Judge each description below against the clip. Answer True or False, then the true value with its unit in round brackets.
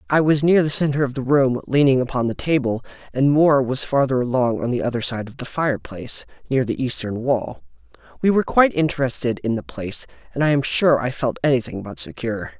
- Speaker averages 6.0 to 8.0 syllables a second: True (6.1 syllables/s)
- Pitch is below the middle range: True (130 Hz)